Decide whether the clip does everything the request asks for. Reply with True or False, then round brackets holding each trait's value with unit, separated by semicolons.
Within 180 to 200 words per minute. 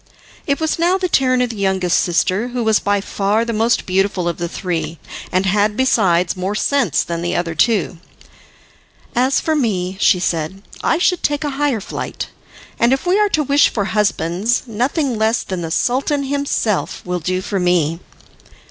True (185 wpm)